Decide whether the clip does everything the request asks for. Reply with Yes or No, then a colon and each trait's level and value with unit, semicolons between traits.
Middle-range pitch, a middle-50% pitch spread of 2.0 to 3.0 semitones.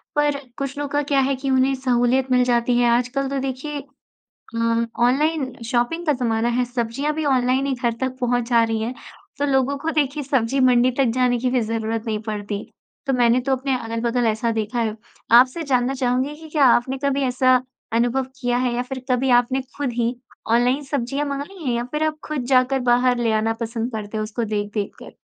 No: very high, 250 Hz; narrow, 2.5 semitones